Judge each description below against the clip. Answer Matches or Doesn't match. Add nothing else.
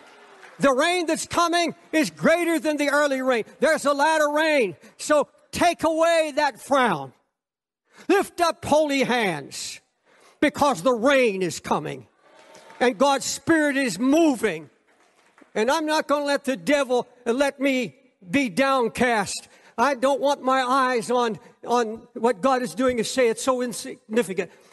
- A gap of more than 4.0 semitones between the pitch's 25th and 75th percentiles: Doesn't match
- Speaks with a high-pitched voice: Matches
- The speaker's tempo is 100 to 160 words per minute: Matches